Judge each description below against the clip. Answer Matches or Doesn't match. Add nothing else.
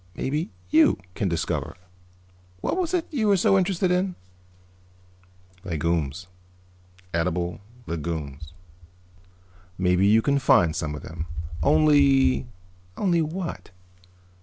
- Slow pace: Matches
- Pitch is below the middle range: Matches